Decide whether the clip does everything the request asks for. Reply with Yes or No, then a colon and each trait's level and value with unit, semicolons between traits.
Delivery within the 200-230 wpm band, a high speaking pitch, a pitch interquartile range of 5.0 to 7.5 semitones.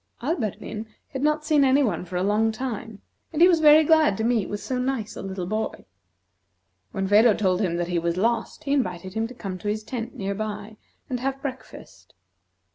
Yes: fast, 205 wpm; high, 220 Hz; average, 5.3 semitones